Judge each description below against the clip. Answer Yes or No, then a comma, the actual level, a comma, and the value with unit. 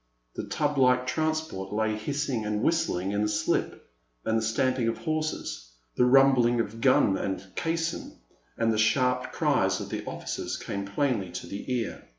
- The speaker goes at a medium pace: Yes, average, 165 wpm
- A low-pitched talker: Yes, low, 120 Hz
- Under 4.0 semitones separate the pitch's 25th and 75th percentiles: No, average, 4.4 semitones